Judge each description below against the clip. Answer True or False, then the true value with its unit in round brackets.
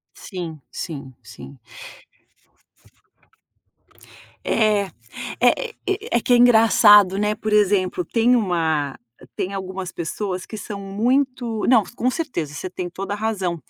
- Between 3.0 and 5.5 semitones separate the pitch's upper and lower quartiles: True (4.0 semitones)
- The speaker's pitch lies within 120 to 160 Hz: False (200 Hz)